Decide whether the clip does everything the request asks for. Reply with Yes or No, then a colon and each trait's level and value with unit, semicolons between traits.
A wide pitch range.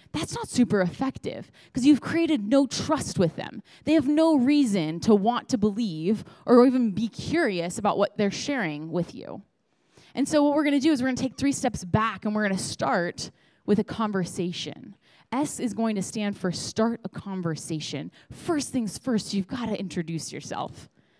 Yes: wide, 5.9 semitones